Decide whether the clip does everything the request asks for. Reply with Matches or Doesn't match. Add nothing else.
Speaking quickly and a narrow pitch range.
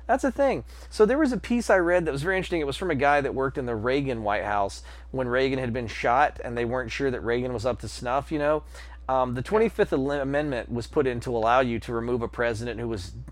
Doesn't match